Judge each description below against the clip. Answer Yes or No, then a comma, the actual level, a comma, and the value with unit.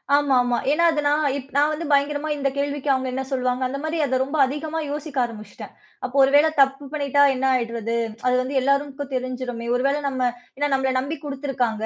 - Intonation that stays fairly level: Yes, narrow, 2.2 semitones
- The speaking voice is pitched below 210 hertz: No, very high, 275 Hz